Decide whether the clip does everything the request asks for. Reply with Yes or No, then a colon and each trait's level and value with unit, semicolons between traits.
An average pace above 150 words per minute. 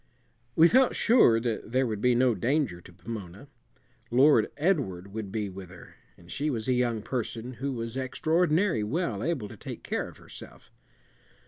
Yes: average, 175 wpm